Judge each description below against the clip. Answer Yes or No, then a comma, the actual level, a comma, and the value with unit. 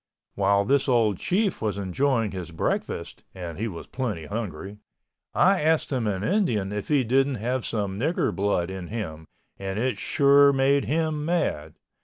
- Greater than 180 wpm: No, average, 165 wpm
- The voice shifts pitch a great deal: Yes, wide, 6.4 semitones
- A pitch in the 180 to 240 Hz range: No, low, 110 Hz